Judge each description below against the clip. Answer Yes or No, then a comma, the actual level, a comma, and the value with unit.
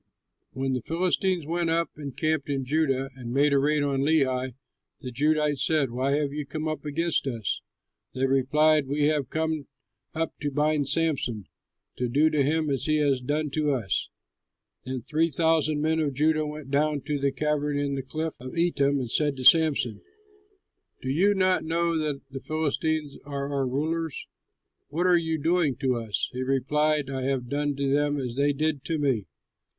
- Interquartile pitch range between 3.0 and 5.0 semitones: No, narrow, 2.6 semitones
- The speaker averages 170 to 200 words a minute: Yes, average, 185 wpm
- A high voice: No, medium, 145 Hz